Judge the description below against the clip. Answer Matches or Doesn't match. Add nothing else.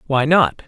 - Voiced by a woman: Doesn't match